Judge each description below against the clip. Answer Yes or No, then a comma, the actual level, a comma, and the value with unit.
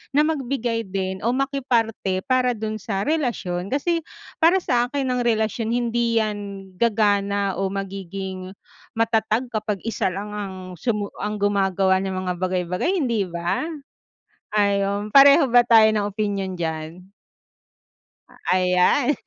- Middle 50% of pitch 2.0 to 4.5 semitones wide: Yes, average, 3.8 semitones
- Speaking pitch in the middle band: No, high, 210 Hz